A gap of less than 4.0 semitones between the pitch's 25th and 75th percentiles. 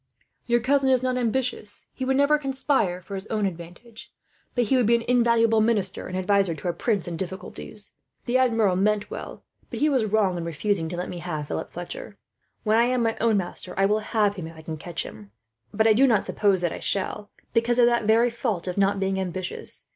No: average, 4.3 semitones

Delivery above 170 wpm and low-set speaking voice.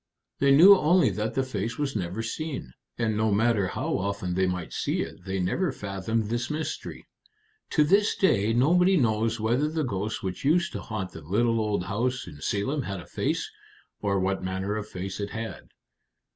Yes: average, 185 wpm; low, 110 Hz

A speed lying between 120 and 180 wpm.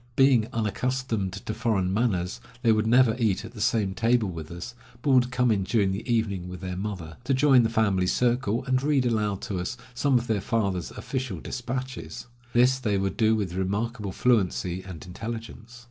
No: average, 190 wpm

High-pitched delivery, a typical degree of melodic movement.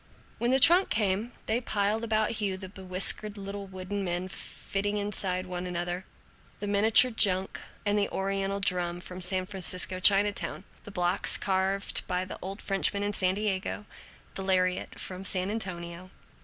No: high, 195 Hz; narrow, 1.9 semitones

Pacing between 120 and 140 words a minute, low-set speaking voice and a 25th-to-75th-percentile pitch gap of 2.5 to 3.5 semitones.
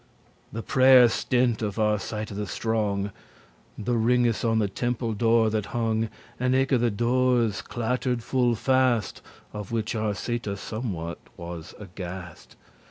Yes: slow, 135 wpm; low, 115 Hz; average, 2.8 semitones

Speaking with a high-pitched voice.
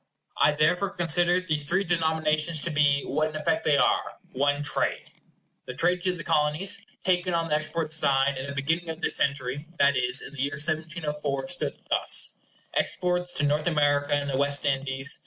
No: medium, 150 Hz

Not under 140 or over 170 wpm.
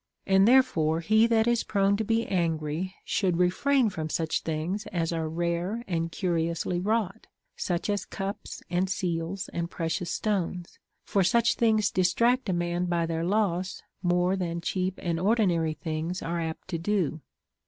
Yes: average, 165 wpm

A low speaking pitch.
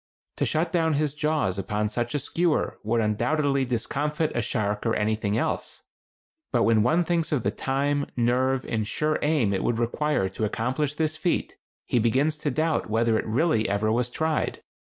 Yes: low, 130 Hz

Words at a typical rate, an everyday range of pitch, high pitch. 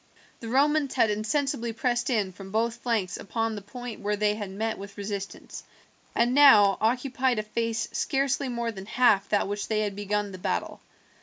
Yes: average, 185 wpm; average, 3.2 semitones; high, 220 Hz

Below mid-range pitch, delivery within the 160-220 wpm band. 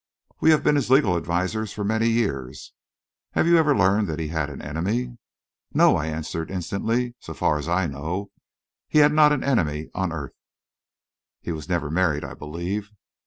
Yes: very low, 95 Hz; average, 180 wpm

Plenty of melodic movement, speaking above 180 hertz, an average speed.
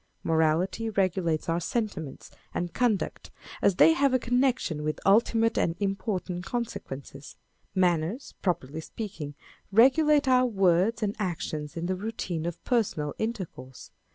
No: wide, 5.8 semitones; high, 190 Hz; slow, 130 wpm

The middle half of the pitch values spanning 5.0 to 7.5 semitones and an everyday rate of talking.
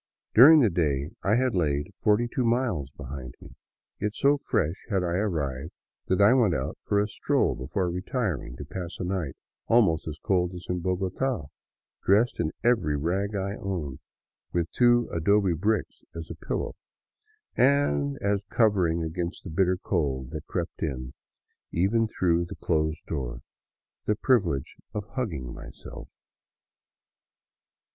Yes: average, 5.3 semitones; average, 150 wpm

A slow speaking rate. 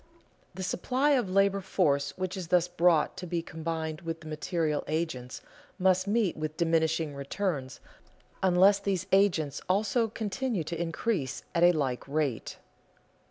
No: average, 145 wpm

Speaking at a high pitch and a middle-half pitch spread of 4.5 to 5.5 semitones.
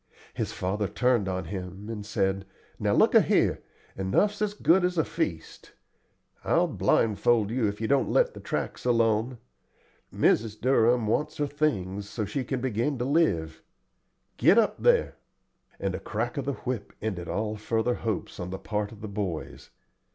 No: low, 110 Hz; average, 5.0 semitones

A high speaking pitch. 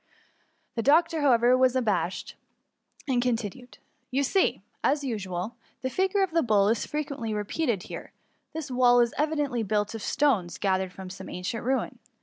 Yes: high, 245 Hz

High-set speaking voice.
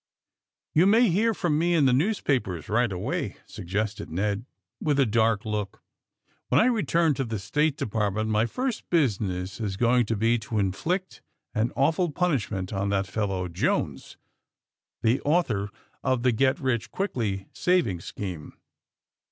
No: low, 115 Hz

